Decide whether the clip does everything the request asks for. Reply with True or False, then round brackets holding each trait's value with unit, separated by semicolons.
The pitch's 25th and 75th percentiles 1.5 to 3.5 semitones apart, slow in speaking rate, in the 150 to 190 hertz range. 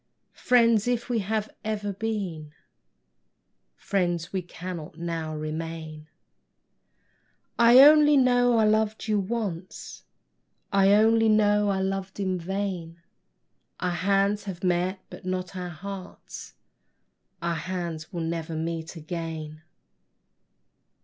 False (4.2 semitones; 110 wpm; 185 Hz)